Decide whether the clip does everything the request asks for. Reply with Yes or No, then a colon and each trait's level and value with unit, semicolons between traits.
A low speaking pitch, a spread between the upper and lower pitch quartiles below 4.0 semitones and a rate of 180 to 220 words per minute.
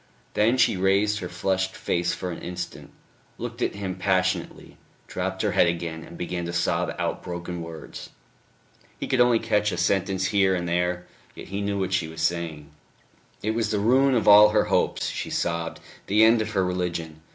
Yes: very low, 95 Hz; average, 3.1 semitones; average, 190 wpm